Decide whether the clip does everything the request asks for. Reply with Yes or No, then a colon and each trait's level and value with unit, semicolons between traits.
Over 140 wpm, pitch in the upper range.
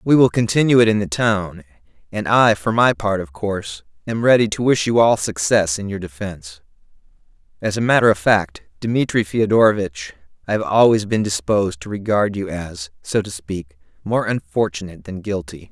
No: average, 175 wpm; low, 100 Hz